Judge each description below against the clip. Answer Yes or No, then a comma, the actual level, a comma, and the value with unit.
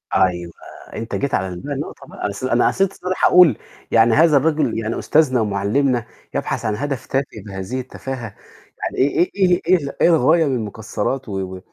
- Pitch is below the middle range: Yes, low, 130 Hz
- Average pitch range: No, wide, 6.6 semitones